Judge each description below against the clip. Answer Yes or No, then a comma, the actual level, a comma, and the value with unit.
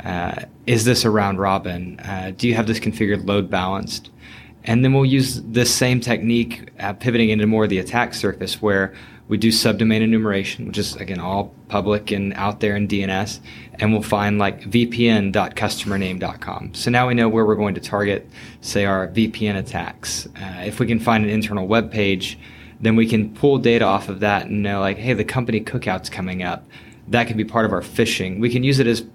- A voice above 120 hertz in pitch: No, low, 110 Hz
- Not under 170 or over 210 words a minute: Yes, fast, 205 wpm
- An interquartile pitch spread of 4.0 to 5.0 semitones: No, average, 2.7 semitones